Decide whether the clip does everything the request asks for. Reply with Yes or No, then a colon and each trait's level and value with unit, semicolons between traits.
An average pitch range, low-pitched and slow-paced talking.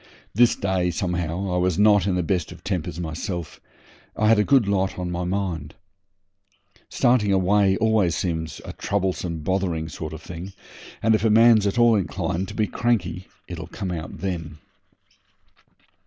No: average, 3.2 semitones; very low, 95 Hz; average, 165 wpm